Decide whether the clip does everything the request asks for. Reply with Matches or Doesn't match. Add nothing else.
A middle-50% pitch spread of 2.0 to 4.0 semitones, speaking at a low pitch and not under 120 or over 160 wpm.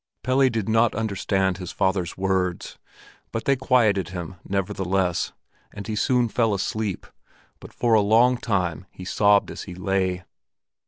Matches